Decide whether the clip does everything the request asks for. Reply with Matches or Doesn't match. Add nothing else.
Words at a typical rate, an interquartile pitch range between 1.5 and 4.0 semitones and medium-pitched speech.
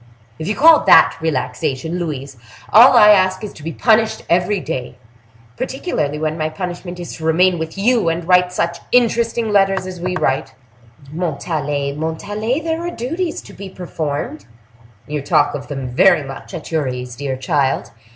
Doesn't match